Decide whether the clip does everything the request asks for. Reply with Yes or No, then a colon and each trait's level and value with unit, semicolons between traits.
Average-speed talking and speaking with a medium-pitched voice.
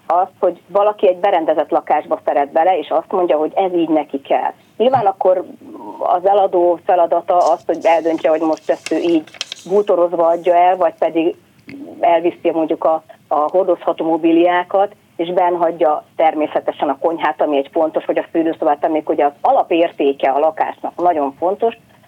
No: fast, 160 wpm; medium, 170 Hz